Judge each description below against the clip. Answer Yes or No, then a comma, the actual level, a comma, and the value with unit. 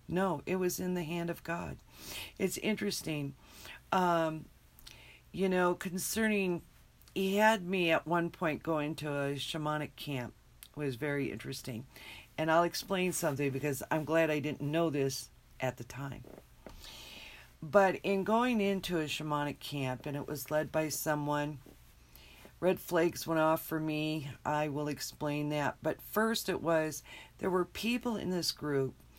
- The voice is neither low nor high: Yes, medium, 155 Hz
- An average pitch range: Yes, average, 3.9 semitones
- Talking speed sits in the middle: Yes, average, 155 wpm